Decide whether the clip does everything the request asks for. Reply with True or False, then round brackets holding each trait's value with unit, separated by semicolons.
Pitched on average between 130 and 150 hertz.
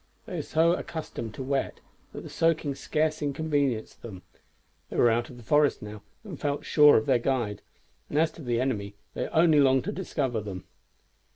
True (135 Hz)